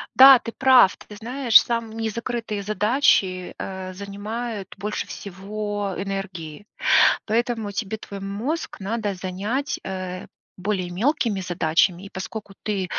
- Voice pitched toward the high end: Yes, high, 205 Hz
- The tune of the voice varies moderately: Yes, average, 3.2 semitones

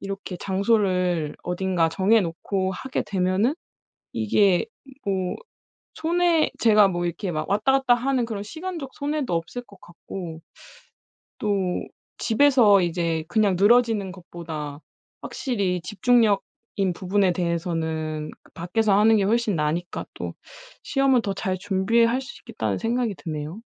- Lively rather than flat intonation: No, average, 4.8 semitones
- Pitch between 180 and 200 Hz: Yes, high, 195 Hz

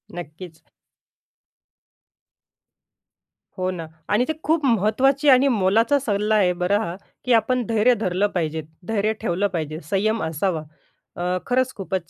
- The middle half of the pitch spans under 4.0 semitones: No, average, 5.1 semitones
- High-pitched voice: Yes, high, 205 Hz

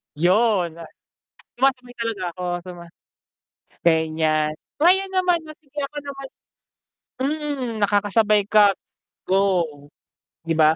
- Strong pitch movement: Yes, wide, 7.9 semitones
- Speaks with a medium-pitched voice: No, high, 210 Hz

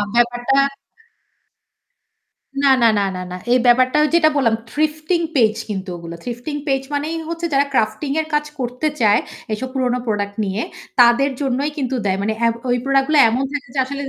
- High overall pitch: Yes, very high, 255 Hz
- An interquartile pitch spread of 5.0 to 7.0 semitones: No, average, 3.8 semitones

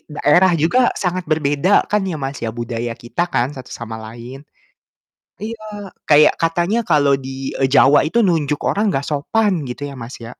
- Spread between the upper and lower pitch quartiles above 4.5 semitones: Yes, average, 5.3 semitones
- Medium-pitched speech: Yes, medium, 145 Hz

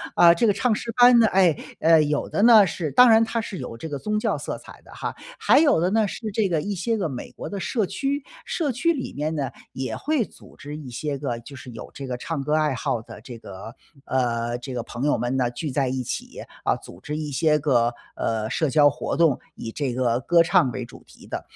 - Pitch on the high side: No, medium, 150 Hz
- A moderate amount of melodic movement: No, wide, 8.0 semitones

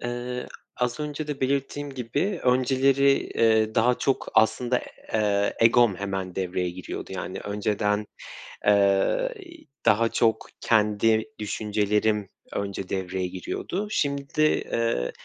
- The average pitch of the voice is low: Yes, low, 110 Hz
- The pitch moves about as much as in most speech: Yes, average, 4.2 semitones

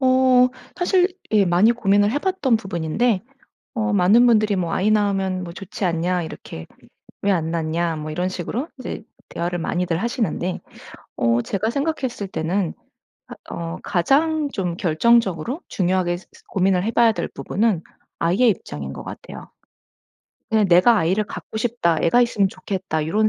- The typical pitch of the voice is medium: No, high, 195 Hz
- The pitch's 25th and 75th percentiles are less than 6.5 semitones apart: Yes, average, 5.2 semitones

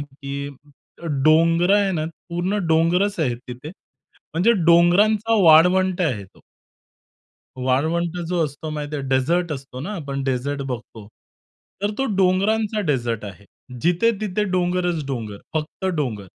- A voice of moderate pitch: Yes, medium, 160 Hz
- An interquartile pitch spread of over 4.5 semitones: Yes, average, 5.0 semitones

